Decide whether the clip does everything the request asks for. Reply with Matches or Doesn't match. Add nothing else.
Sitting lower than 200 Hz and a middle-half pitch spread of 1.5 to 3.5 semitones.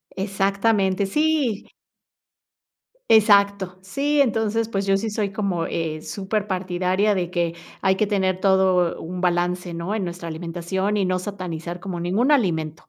Matches